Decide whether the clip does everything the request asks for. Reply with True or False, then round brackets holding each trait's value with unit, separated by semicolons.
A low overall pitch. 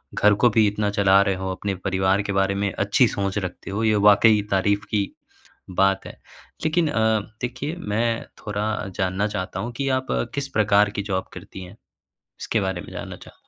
True (100 Hz)